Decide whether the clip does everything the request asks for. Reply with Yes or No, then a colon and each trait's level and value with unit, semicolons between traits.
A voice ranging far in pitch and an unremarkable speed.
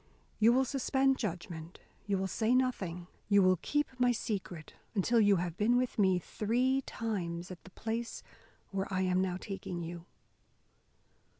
No: average, 4.8 semitones; average, 160 wpm